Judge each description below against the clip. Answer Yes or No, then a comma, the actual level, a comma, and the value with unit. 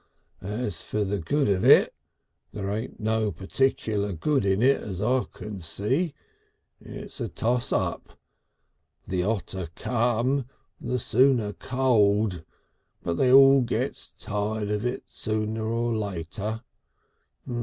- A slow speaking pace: Yes, slow, 125 wpm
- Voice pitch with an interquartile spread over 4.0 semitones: No, average, 3.5 semitones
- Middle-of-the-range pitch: No, low, 110 Hz